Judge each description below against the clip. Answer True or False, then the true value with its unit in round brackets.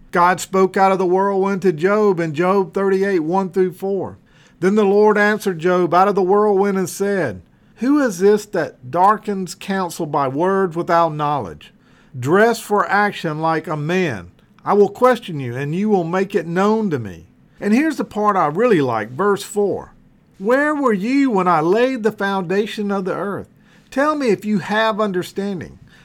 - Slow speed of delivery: False (180 wpm)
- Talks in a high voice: True (195 Hz)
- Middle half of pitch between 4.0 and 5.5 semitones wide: False (2.6 semitones)